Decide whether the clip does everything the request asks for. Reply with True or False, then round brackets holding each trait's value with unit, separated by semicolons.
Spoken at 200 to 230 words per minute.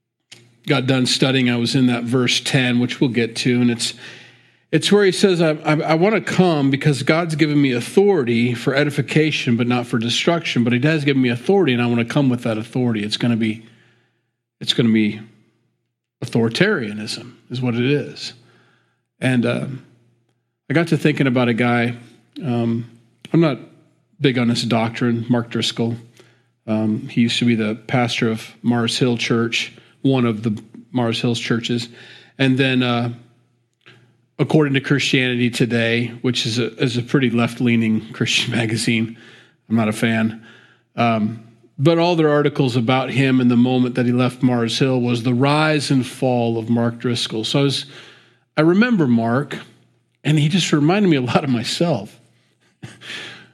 False (175 wpm)